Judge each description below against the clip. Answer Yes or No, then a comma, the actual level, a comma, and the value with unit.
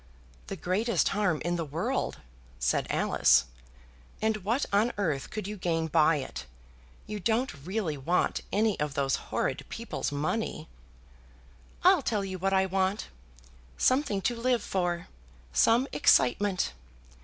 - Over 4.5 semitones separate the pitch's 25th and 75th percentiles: Yes, average, 5.0 semitones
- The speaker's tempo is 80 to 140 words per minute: Yes, slow, 135 wpm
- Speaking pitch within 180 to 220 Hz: Yes, high, 190 Hz